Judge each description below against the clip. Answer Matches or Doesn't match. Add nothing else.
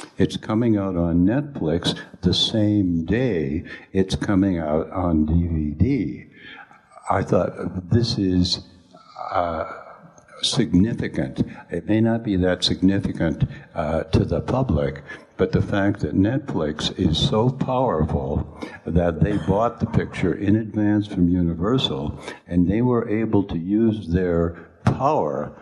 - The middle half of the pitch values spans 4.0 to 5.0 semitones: Doesn't match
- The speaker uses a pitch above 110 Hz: Doesn't match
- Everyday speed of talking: Doesn't match